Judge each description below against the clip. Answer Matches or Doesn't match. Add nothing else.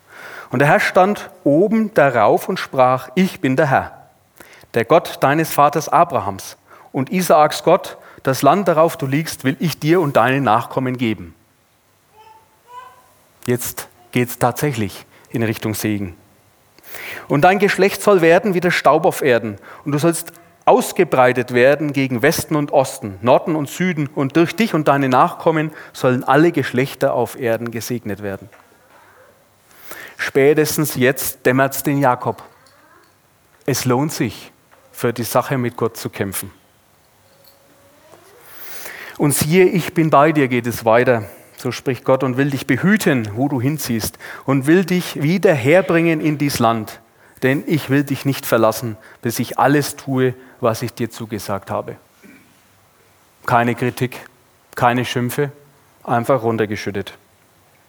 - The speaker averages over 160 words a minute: Doesn't match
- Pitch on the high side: Doesn't match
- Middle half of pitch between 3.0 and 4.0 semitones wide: Doesn't match